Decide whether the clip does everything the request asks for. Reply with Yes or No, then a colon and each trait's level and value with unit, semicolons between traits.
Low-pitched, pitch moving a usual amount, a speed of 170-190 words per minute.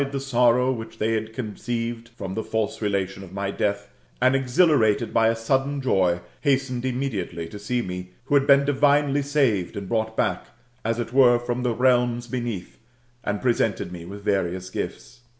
Yes: low, 115 Hz; average, 4.2 semitones; average, 185 wpm